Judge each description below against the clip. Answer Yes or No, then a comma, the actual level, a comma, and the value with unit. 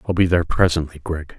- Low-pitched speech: Yes, very low, 85 Hz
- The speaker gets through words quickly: Yes, fast, 215 wpm